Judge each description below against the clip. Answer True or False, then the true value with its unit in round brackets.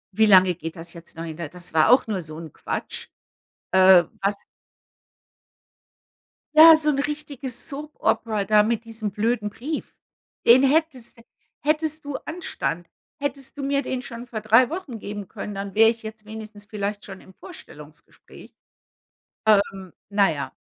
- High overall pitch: True (220 Hz)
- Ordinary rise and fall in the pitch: False (6.0 semitones)